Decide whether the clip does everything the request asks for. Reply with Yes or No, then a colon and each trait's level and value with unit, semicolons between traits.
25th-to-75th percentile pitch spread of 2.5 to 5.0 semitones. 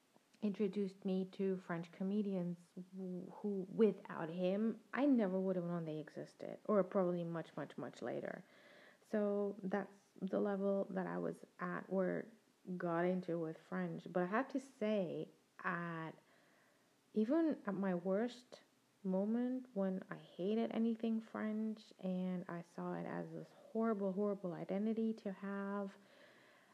Yes: average, 2.9 semitones